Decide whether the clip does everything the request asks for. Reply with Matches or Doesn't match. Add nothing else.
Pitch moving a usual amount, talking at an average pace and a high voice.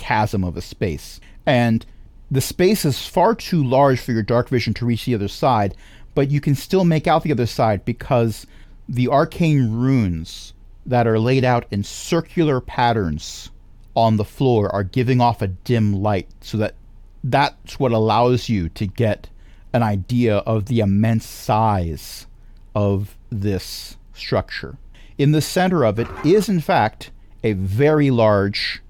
Doesn't match